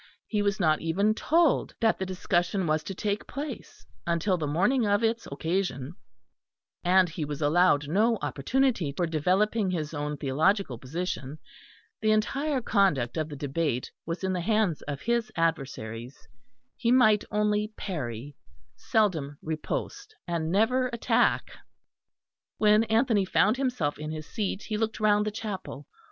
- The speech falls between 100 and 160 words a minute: Yes, average, 145 wpm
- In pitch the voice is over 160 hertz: Yes, medium, 185 Hz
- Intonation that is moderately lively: No, wide, 5.9 semitones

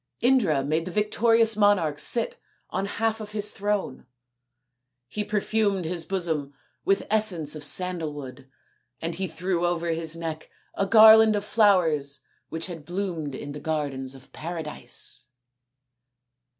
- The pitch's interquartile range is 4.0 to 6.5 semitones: Yes, average, 5.1 semitones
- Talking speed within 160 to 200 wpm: No, slow, 135 wpm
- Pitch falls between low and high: Yes, medium, 175 Hz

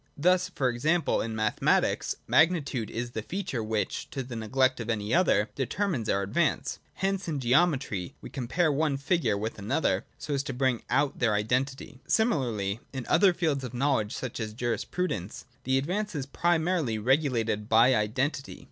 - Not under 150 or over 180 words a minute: Yes, average, 165 wpm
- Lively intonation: Yes, wide, 6.0 semitones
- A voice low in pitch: Yes, low, 130 Hz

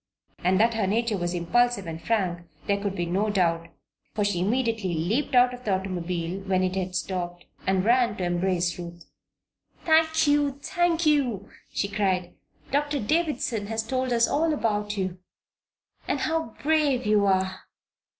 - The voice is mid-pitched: No, high, 205 Hz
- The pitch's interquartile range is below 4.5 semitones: No, wide, 5.4 semitones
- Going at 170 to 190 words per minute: No, average, 160 wpm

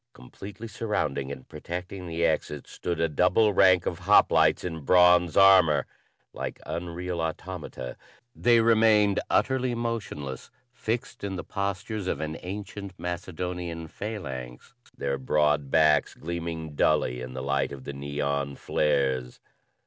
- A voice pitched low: Yes, very low, 85 Hz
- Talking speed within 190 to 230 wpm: No, slow, 135 wpm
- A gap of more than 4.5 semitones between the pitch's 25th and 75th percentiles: Yes, wide, 5.5 semitones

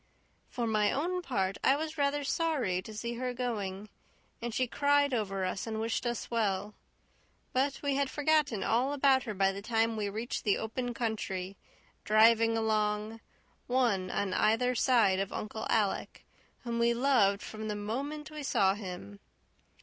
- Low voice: No, high, 225 Hz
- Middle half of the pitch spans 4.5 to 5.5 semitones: No, average, 4.1 semitones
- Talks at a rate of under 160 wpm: No, average, 165 wpm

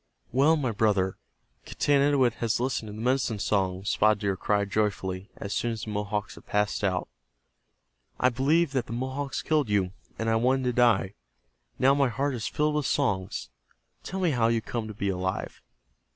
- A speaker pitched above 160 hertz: No, low, 115 Hz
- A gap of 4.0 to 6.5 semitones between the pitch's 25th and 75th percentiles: Yes, average, 4.6 semitones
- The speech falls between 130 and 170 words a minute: No, average, 180 wpm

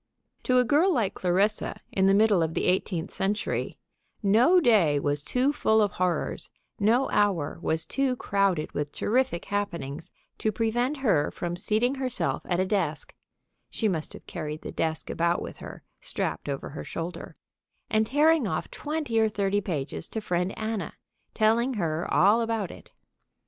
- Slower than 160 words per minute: No, average, 165 wpm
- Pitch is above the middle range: Yes, high, 205 Hz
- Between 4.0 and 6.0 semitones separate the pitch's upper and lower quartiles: Yes, average, 5.2 semitones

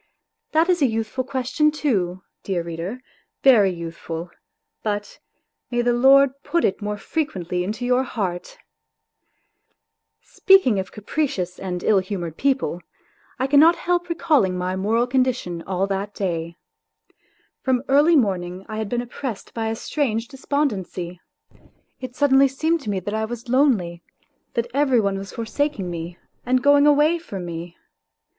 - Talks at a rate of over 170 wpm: No, average, 145 wpm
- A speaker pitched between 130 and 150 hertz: No, high, 225 Hz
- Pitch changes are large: Yes, wide, 6.6 semitones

